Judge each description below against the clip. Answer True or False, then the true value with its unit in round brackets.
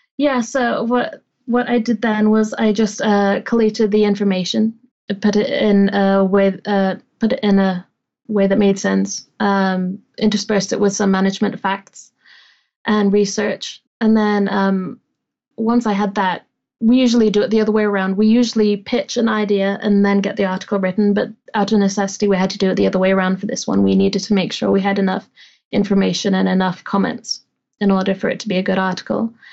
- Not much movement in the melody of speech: True (2.2 semitones)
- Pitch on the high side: True (205 Hz)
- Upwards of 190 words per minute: True (205 wpm)